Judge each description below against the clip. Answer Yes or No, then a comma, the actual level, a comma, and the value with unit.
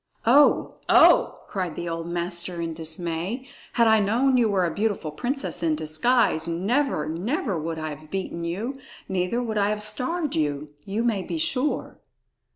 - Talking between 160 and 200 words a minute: Yes, average, 165 wpm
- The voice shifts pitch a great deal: Yes, wide, 6.4 semitones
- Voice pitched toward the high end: Yes, high, 195 Hz